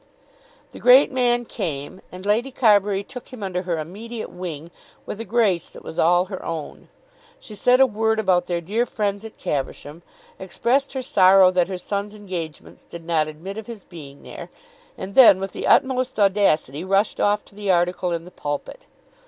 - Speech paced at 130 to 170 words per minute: No, average, 185 wpm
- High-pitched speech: Yes, high, 195 Hz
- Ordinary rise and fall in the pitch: Yes, average, 4.2 semitones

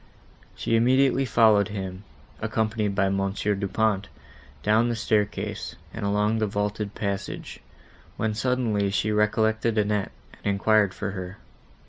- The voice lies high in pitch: No, low, 105 Hz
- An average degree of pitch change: No, narrow, 1.7 semitones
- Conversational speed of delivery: No, slow, 130 wpm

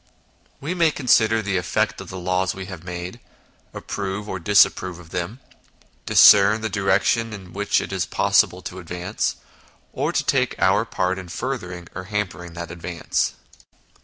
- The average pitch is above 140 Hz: No, very low, 95 Hz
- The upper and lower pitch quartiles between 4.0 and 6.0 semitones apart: No, average, 2.8 semitones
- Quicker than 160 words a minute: No, average, 155 wpm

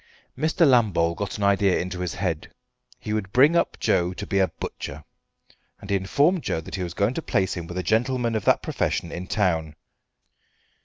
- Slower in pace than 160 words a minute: No, average, 200 wpm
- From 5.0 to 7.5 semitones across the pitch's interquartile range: No, average, 4.4 semitones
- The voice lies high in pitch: No, low, 100 Hz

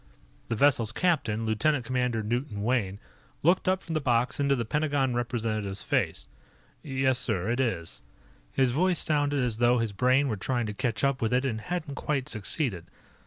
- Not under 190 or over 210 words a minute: No, average, 175 wpm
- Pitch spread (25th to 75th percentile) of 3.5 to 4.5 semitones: Yes, average, 4.1 semitones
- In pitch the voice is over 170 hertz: No, low, 125 Hz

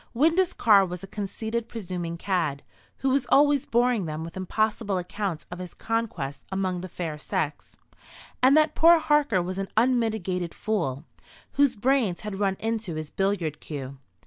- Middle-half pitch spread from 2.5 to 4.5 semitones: No, average, 5.2 semitones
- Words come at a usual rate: Yes, average, 160 wpm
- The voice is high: Yes, high, 195 Hz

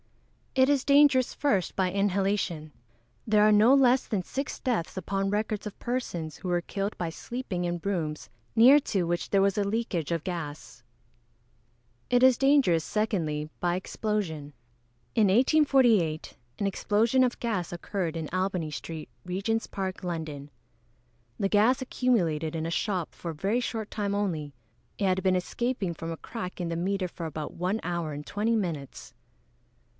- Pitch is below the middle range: No, high, 195 Hz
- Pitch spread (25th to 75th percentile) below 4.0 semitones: No, average, 4.9 semitones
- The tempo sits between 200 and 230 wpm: No, average, 165 wpm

